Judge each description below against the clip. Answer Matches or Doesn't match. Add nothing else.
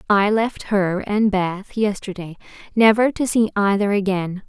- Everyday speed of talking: Matches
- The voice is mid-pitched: Doesn't match